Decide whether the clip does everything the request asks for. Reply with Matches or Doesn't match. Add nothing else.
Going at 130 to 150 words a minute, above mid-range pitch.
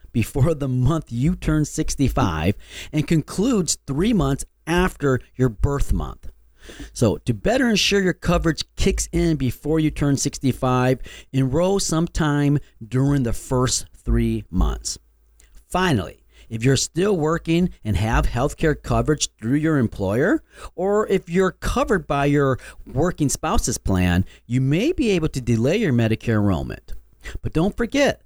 Doesn't match